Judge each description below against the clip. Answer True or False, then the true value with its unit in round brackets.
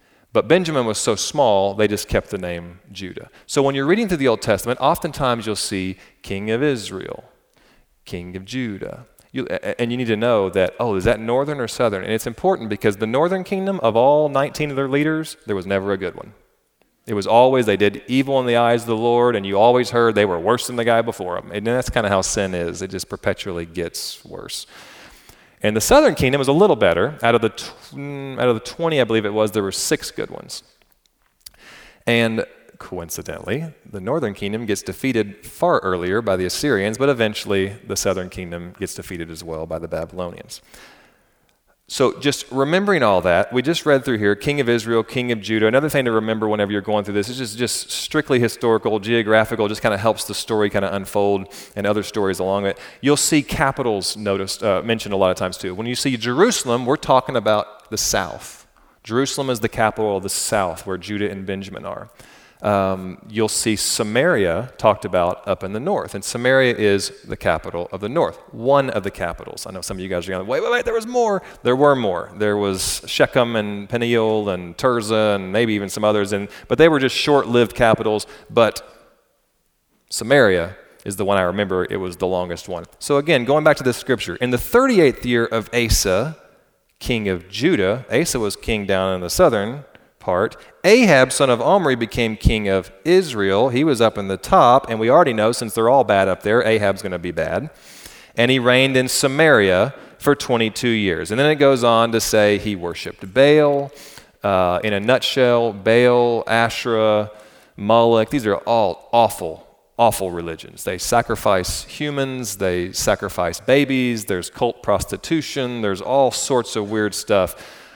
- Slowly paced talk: False (200 wpm)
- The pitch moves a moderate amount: True (4.4 semitones)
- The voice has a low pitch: True (110 Hz)